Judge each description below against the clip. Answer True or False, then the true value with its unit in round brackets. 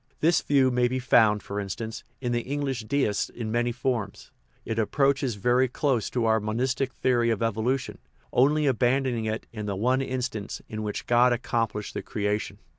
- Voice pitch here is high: False (120 Hz)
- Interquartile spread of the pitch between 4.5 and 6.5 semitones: False (3.0 semitones)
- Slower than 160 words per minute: False (175 wpm)